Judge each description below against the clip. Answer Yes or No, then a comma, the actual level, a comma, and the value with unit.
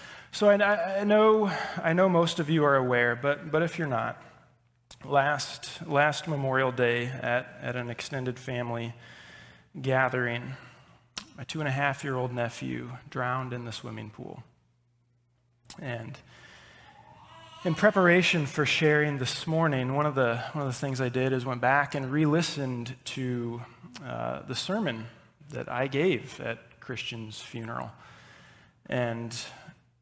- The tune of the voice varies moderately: Yes, average, 3.7 semitones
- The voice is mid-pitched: No, low, 130 Hz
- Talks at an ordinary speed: Yes, average, 145 wpm